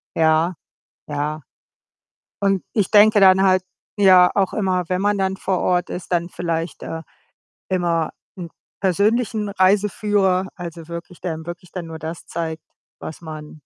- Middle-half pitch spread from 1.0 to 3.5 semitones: Yes, average, 2.7 semitones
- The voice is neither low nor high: Yes, medium, 180 Hz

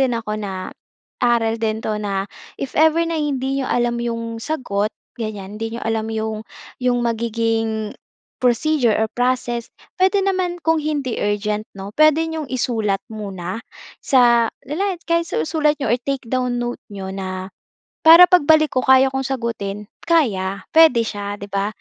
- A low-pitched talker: No, high, 235 Hz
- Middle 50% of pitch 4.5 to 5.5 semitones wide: Yes, average, 4.9 semitones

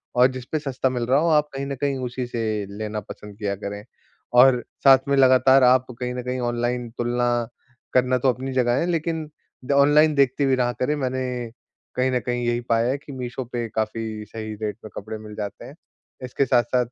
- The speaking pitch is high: No, low, 125 Hz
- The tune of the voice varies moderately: No, narrow, 2.1 semitones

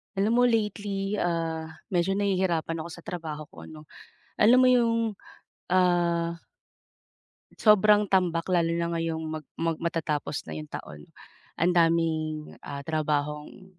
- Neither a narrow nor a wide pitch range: Yes, average, 3.5 semitones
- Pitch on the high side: No, medium, 170 Hz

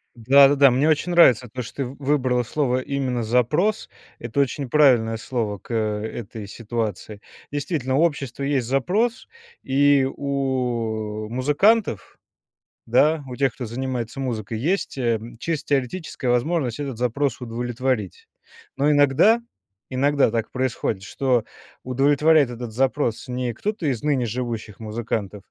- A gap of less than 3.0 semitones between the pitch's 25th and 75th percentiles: No, average, 3.6 semitones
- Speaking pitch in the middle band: No, low, 130 Hz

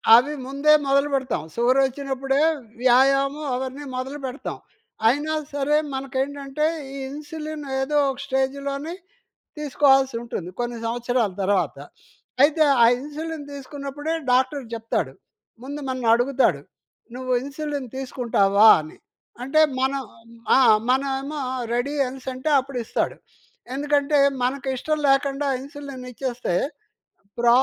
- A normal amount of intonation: No, narrow, 2.0 semitones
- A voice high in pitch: Yes, very high, 270 Hz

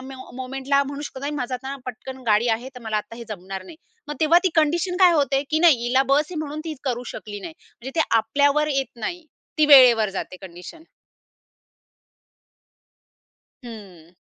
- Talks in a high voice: Yes, very high, 265 Hz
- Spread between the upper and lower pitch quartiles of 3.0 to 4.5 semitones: No, average, 5.0 semitones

